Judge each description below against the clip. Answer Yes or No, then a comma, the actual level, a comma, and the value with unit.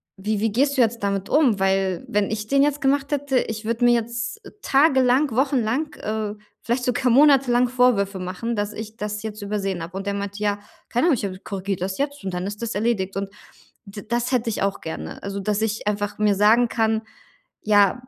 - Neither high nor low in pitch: No, high, 220 Hz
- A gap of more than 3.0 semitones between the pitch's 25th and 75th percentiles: Yes, average, 3.7 semitones